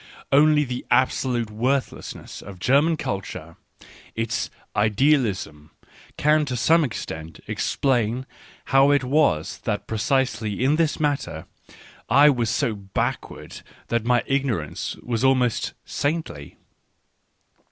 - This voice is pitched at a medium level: No, low, 125 Hz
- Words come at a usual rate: No, slow, 130 wpm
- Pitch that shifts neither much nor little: Yes, average, 4.8 semitones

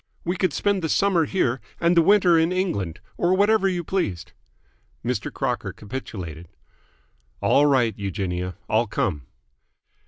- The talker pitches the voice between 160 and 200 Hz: No, medium, 145 Hz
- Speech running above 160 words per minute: No, slow, 135 wpm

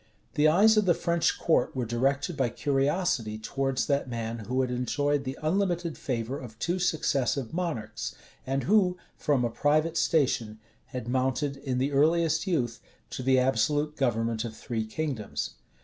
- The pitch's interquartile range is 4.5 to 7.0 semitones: Yes, average, 4.8 semitones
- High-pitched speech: No, low, 135 Hz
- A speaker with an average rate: Yes, average, 160 wpm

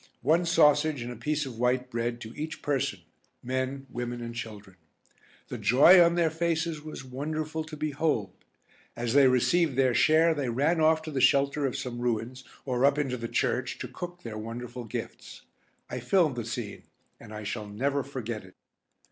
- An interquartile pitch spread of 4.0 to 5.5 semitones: Yes, average, 4.4 semitones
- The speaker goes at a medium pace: Yes, average, 180 wpm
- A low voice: Yes, low, 130 Hz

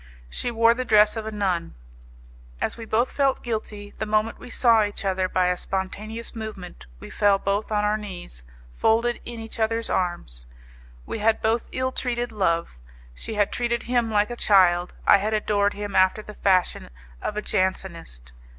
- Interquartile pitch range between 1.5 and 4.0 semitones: Yes, average, 3.2 semitones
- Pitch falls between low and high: No, high, 210 Hz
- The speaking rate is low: No, average, 180 wpm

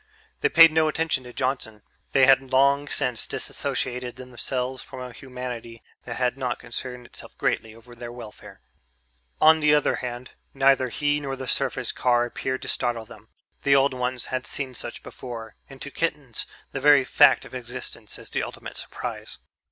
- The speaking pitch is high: No, low, 130 Hz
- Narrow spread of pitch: Yes, narrow, 2.1 semitones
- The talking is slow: No, average, 175 wpm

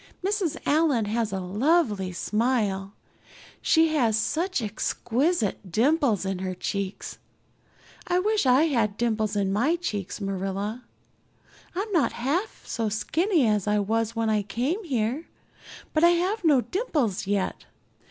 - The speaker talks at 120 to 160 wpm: Yes, slow, 135 wpm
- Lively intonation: Yes, wide, 7.8 semitones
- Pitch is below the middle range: No, high, 230 Hz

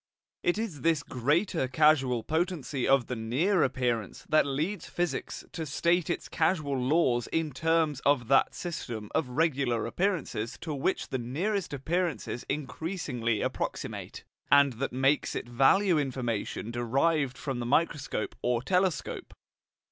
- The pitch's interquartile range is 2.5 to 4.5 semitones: No, average, 4.9 semitones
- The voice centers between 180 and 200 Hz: No, medium, 140 Hz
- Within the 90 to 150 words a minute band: Yes, slow, 135 wpm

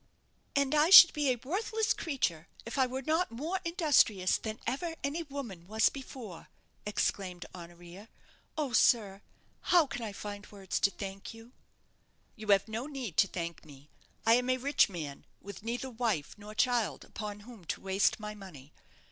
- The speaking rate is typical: Yes, average, 170 wpm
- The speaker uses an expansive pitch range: Yes, wide, 5.8 semitones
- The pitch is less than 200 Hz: No, high, 220 Hz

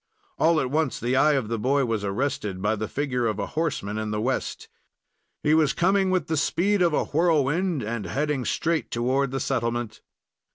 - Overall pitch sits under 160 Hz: Yes, low, 135 Hz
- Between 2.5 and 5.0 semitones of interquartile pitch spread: No, wide, 5.5 semitones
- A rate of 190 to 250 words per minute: Yes, average, 195 wpm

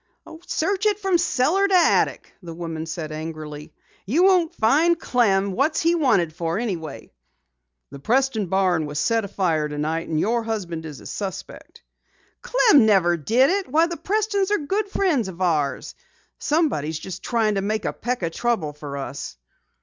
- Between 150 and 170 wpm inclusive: Yes, average, 165 wpm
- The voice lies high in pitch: Yes, high, 210 Hz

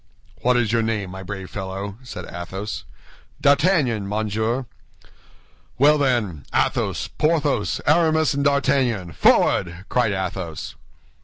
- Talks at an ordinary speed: No, slow, 110 wpm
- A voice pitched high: No, low, 110 Hz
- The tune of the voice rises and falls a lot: Yes, wide, 6.6 semitones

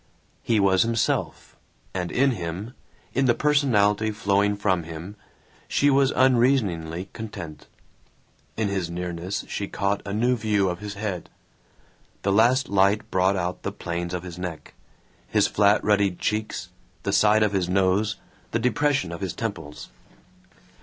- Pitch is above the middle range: No, low, 100 Hz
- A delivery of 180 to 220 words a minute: No, average, 145 wpm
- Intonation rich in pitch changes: No, average, 3.4 semitones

